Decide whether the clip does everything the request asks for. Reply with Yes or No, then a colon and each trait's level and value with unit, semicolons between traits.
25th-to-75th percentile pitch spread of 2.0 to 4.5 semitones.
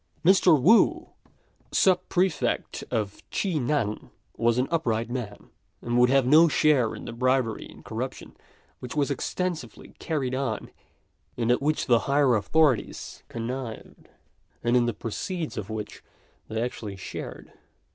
No: average, 4.9 semitones